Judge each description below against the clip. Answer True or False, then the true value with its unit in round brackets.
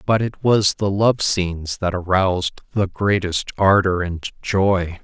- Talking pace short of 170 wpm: True (155 wpm)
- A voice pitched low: True (95 Hz)